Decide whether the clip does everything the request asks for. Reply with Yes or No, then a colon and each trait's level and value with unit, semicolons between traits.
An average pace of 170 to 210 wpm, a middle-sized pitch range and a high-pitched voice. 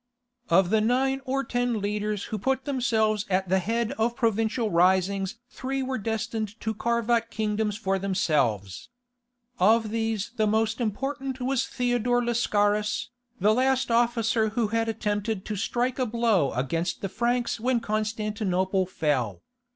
No: average, 145 wpm; average, 3.1 semitones; high, 220 Hz